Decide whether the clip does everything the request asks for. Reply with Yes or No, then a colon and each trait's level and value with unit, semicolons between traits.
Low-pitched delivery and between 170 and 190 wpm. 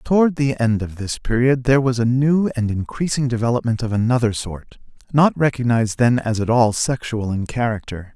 Yes: low, 120 Hz; average, 185 wpm